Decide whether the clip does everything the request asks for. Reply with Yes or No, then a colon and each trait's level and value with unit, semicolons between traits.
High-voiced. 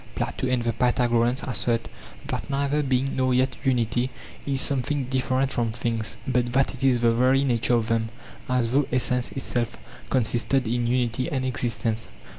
No: low, 125 Hz